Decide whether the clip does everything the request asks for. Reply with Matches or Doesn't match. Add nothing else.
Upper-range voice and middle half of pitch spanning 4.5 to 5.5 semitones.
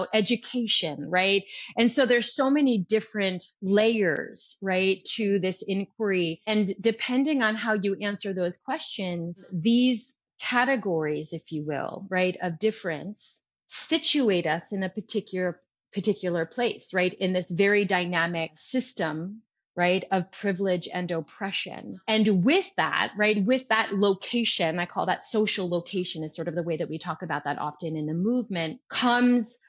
Doesn't match